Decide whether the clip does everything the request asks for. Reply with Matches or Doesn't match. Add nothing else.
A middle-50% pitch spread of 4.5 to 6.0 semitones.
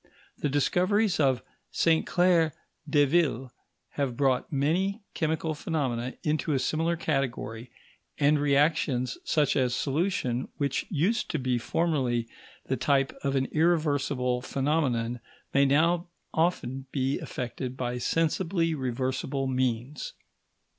Doesn't match